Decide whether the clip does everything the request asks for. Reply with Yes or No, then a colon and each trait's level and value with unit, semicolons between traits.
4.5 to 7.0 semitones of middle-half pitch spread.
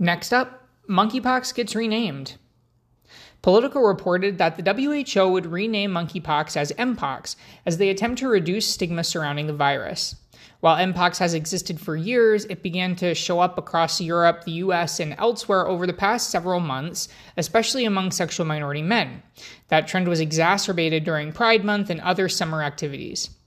No: average, 3.8 semitones